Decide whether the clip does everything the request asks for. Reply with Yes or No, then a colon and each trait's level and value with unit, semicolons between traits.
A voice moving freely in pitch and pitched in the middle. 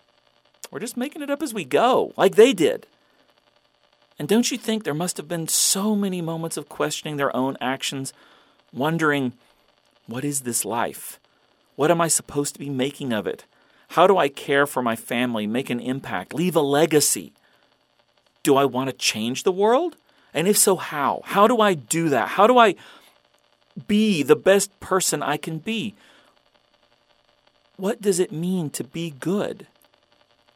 Yes: wide, 7.1 semitones; medium, 160 Hz